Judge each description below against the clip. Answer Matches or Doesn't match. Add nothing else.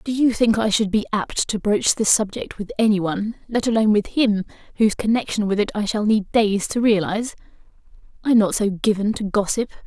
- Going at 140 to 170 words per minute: Doesn't match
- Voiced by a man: Doesn't match